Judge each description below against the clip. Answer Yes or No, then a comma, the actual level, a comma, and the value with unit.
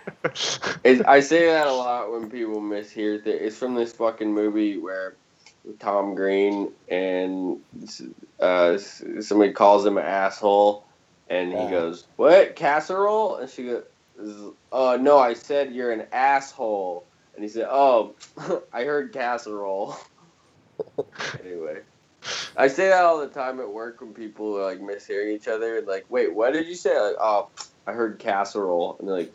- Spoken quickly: No, average, 160 wpm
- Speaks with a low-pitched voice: Yes, low, 110 Hz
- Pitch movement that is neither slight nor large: No, wide, 5.8 semitones